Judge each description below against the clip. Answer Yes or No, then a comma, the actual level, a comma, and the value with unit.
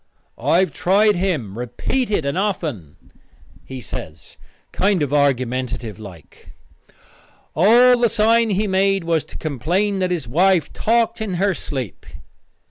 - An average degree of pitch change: No, wide, 7.9 semitones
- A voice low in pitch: No, medium, 180 Hz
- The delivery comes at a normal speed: No, slow, 130 wpm